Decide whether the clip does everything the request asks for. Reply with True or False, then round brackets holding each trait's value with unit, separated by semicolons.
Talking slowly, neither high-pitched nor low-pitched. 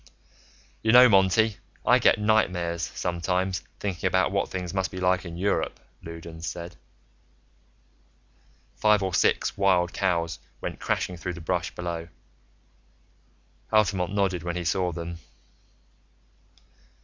False (125 wpm; 90 Hz)